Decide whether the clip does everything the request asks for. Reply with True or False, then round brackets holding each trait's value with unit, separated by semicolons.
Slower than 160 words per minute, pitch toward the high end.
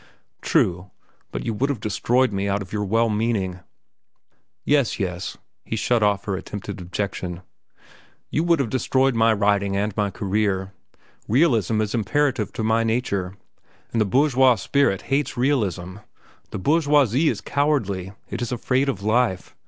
False (150 wpm; 110 Hz)